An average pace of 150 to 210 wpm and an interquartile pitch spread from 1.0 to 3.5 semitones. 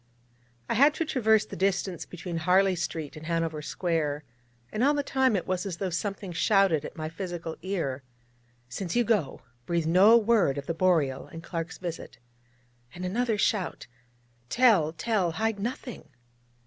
No: average, 160 wpm; average, 4.7 semitones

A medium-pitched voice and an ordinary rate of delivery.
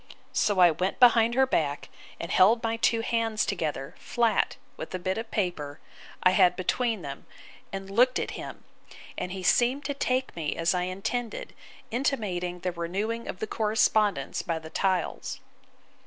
No: high, 195 Hz; average, 165 wpm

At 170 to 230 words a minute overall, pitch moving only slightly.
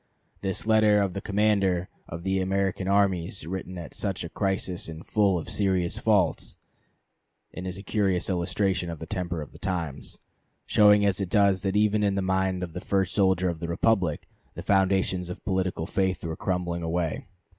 Yes: average, 185 wpm; narrow, 2.1 semitones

